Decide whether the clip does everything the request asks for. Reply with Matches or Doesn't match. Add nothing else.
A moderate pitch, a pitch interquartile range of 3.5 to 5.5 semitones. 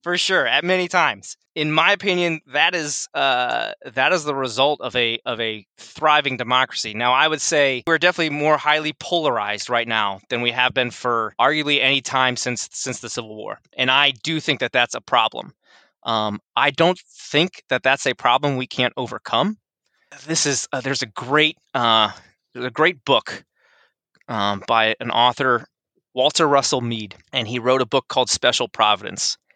Doesn't match